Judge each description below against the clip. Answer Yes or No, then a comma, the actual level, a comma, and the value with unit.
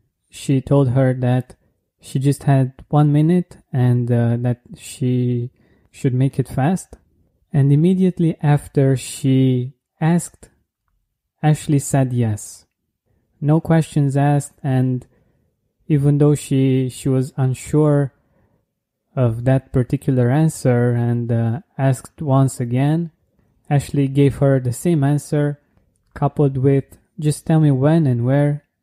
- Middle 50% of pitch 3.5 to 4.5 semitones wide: No, average, 3.0 semitones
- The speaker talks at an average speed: No, slow, 120 wpm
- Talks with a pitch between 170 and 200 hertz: No, low, 135 Hz